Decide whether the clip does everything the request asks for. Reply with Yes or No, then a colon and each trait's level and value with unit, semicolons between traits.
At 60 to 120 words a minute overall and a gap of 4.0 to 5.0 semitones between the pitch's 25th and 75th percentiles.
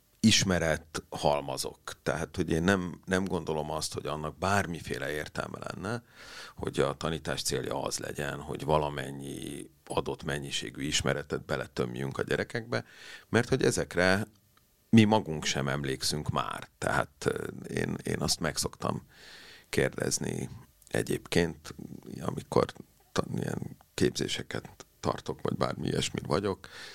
Yes: average, 115 wpm; average, 4.5 semitones